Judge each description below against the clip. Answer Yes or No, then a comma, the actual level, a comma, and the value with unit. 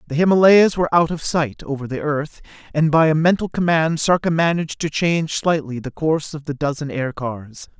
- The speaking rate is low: No, average, 195 wpm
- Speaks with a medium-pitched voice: Yes, medium, 155 Hz